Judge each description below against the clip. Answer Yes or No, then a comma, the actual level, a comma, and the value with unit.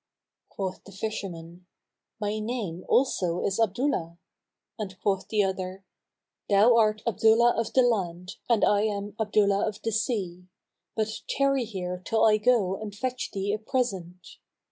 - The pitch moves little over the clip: No, average, 3.1 semitones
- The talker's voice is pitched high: Yes, high, 205 Hz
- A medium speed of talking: Yes, average, 145 wpm